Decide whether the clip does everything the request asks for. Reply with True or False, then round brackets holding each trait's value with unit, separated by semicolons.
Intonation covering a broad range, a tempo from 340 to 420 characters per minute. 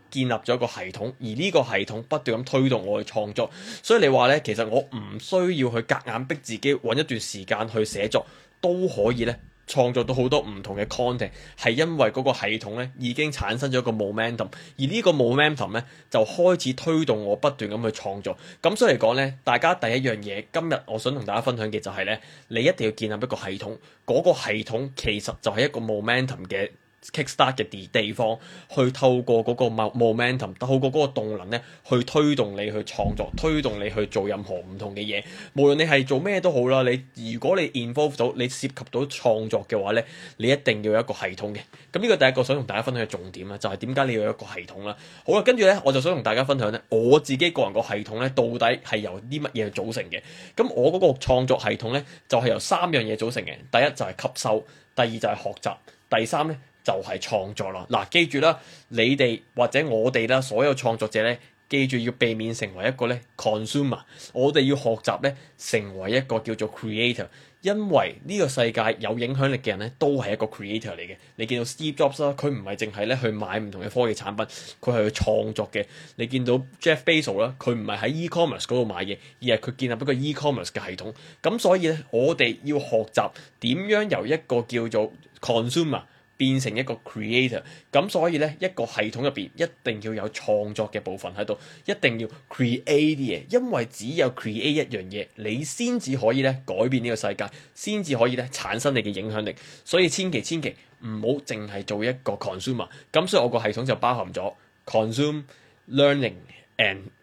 False (4.4 semitones; 380 characters per minute)